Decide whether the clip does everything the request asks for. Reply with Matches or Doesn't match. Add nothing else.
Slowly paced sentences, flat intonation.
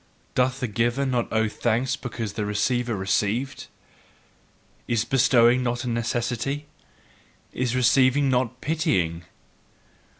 Matches